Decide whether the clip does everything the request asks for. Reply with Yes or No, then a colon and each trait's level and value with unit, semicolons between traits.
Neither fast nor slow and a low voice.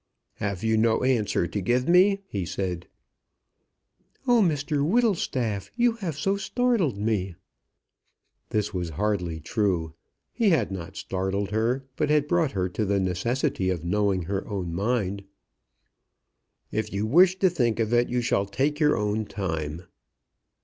Yes: average, 150 wpm; low, 110 Hz